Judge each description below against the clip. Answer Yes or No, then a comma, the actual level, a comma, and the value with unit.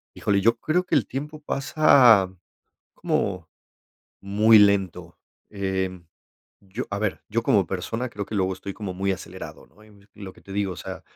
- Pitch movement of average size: Yes, average, 3.0 semitones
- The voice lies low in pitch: Yes, low, 100 Hz